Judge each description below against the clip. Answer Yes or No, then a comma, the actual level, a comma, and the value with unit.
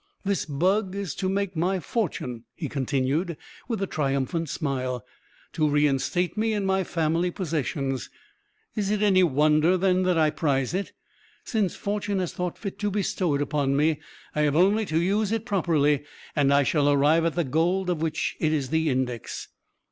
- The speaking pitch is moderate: Yes, medium, 165 Hz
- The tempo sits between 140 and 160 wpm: No, average, 180 wpm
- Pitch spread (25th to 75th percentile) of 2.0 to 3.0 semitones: No, average, 4.8 semitones